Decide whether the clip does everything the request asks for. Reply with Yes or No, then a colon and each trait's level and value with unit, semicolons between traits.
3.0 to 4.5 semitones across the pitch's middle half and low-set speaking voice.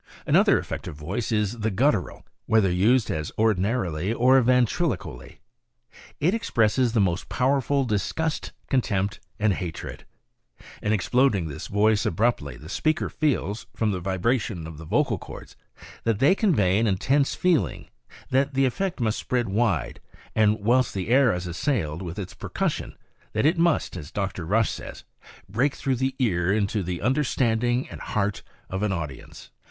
No: wide, 5.5 semitones; low, 110 Hz